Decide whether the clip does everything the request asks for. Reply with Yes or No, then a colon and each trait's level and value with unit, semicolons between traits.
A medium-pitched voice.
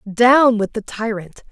No: high, 225 Hz